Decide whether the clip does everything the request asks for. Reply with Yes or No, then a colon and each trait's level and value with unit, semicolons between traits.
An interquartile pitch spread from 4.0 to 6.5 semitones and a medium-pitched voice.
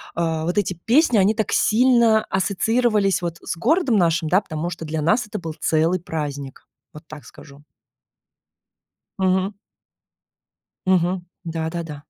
Yes: average, 4.8 semitones; medium, 180 Hz